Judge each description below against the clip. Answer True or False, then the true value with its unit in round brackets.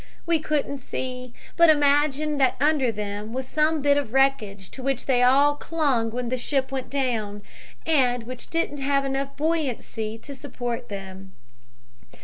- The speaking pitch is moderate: False (265 Hz)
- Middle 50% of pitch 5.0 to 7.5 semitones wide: False (3.3 semitones)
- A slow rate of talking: False (155 wpm)